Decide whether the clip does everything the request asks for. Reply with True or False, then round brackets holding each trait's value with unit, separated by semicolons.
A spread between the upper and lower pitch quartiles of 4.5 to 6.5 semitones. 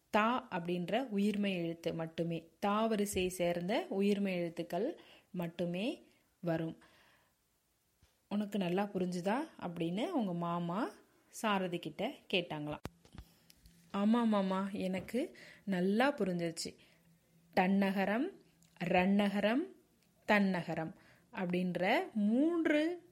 False (3.5 semitones)